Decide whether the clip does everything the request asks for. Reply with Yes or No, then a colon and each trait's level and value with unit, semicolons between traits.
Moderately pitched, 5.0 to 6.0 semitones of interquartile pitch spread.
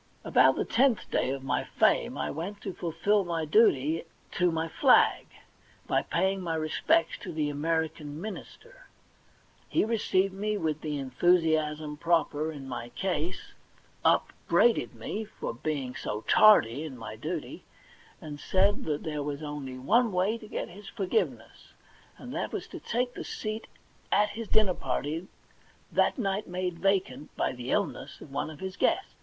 Yes: medium, 165 Hz; wide, 5.4 semitones